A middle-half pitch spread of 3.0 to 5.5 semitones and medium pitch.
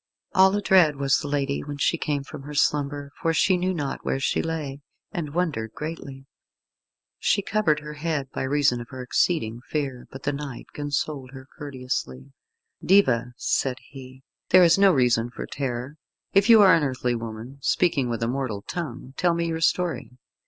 Yes: average, 4.2 semitones; medium, 145 Hz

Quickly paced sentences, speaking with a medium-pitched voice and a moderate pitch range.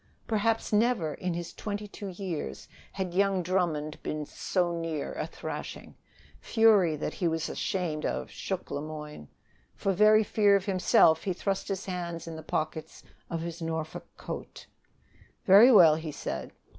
No: average, 155 wpm; medium, 175 Hz; average, 3.9 semitones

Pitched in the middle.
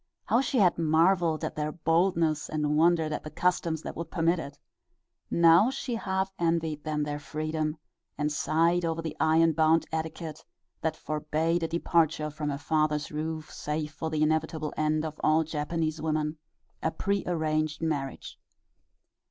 Yes: medium, 160 Hz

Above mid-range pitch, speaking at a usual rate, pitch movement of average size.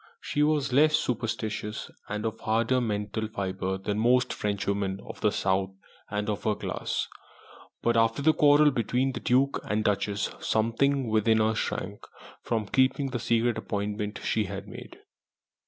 No: low, 110 Hz; average, 155 wpm; average, 3.4 semitones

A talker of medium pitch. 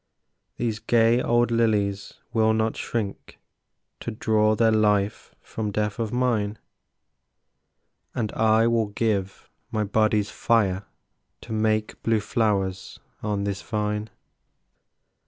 No: low, 110 Hz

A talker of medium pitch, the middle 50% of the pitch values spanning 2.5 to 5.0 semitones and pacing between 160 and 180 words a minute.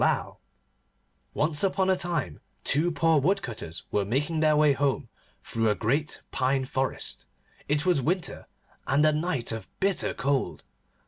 No: medium, 145 Hz; average, 4.2 semitones; average, 145 wpm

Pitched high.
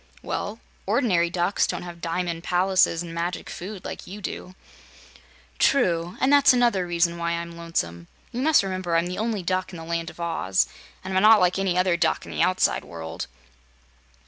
No: medium, 180 Hz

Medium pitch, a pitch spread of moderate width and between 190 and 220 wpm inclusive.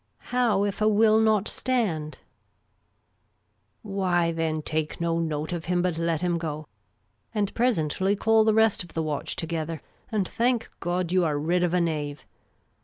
No: medium, 175 Hz; average, 4.7 semitones; average, 180 wpm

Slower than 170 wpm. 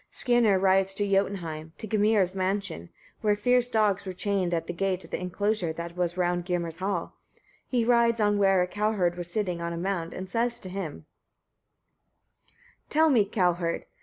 No: average, 185 wpm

